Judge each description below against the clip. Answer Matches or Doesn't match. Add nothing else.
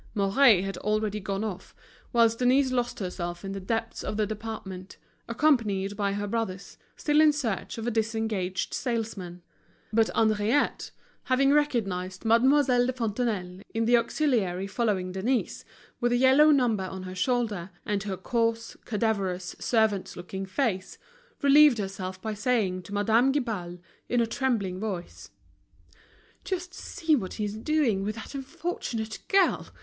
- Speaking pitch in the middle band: Doesn't match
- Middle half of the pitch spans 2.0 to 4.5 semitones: Matches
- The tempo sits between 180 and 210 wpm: Doesn't match